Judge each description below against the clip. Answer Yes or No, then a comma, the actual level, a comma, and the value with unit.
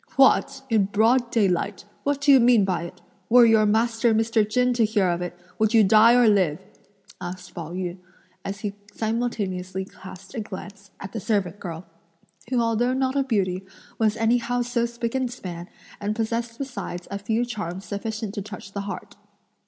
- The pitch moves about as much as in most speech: Yes, average, 3.7 semitones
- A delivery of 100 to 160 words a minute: No, average, 180 wpm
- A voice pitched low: No, high, 215 Hz